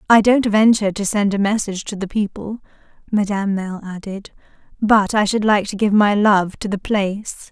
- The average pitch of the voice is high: Yes, high, 205 Hz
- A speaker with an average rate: Yes, average, 190 wpm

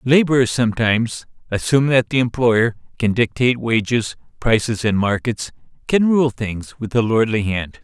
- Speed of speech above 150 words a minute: No, average, 145 wpm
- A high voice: No, low, 115 Hz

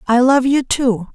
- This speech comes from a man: No, female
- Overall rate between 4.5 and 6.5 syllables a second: No, 4.2 syllables/s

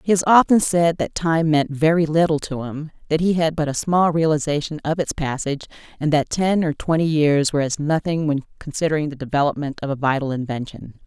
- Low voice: No, medium, 155 Hz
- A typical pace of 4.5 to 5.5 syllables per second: No, 5.7 syllables/s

